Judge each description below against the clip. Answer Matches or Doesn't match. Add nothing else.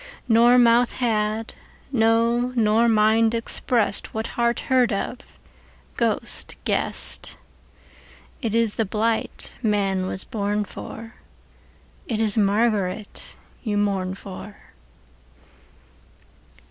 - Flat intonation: Matches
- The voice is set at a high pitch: Matches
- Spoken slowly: Matches